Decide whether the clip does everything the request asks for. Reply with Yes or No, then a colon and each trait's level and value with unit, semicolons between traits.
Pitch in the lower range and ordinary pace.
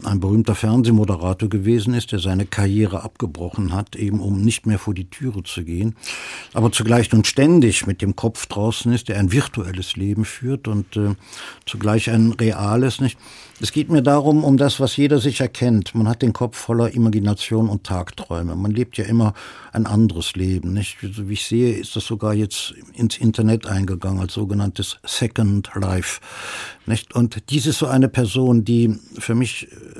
Yes: low, 110 Hz; average, 180 wpm